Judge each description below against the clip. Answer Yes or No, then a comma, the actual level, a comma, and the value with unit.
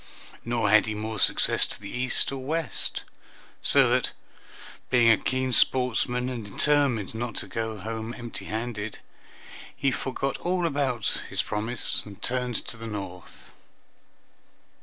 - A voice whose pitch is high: No, low, 120 Hz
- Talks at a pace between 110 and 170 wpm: Yes, average, 140 wpm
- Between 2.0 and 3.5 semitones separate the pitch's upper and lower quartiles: Yes, average, 2.9 semitones